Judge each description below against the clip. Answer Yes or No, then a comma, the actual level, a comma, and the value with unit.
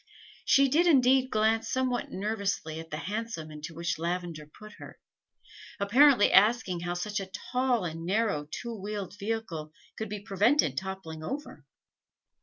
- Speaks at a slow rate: No, average, 145 wpm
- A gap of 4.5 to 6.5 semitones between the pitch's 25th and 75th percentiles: Yes, average, 5.3 semitones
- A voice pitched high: Yes, high, 205 Hz